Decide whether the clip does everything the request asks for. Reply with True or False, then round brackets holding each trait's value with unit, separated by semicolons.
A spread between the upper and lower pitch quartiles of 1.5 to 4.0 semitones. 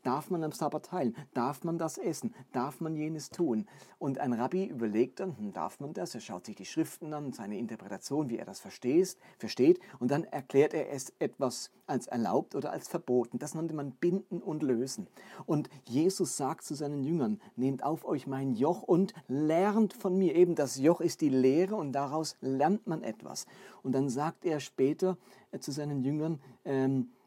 False (5.1 semitones)